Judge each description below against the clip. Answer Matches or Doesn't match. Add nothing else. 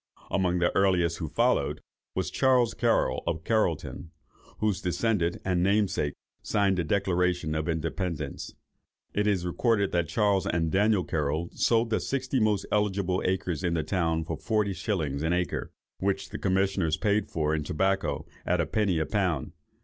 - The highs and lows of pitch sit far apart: Doesn't match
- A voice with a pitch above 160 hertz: Doesn't match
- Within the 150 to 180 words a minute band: Matches